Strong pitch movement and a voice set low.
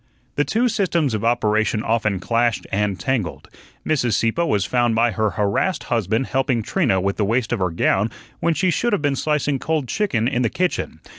Yes: wide, 5.8 semitones; low, 120 Hz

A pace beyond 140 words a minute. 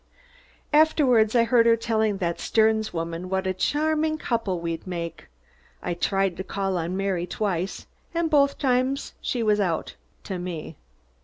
Yes: average, 155 wpm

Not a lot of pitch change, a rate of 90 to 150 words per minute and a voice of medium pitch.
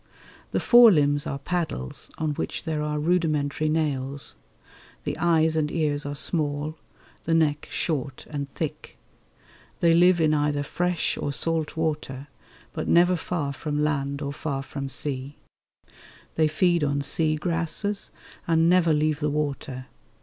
Yes: narrow, 2.3 semitones; average, 145 wpm; medium, 150 Hz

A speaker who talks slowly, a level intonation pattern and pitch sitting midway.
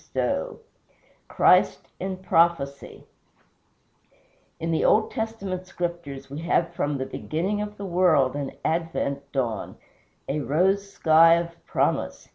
No: slow, 120 wpm; average, 4.6 semitones; medium, 170 Hz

